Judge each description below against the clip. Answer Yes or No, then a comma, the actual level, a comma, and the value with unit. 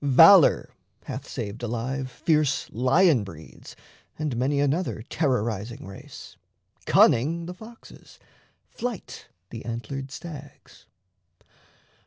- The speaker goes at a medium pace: No, slow, 95 wpm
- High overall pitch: No, low, 135 Hz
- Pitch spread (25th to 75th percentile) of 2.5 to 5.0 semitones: No, wide, 5.5 semitones